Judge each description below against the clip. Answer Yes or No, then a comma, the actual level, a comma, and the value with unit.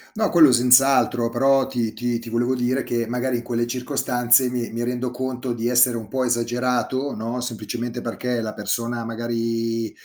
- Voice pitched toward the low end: Yes, low, 120 Hz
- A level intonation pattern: Yes, narrow, 1.4 semitones